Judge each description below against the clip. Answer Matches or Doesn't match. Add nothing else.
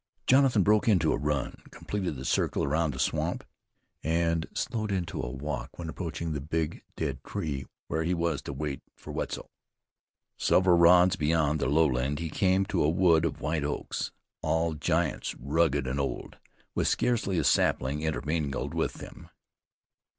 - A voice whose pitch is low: Matches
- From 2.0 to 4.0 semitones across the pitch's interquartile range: Matches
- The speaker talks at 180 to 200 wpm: Doesn't match